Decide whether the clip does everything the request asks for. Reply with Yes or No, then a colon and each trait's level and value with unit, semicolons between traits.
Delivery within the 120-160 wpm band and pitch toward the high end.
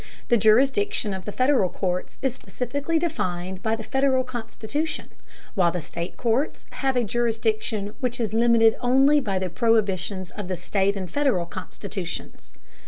Yes: average, 155 wpm; high, 225 Hz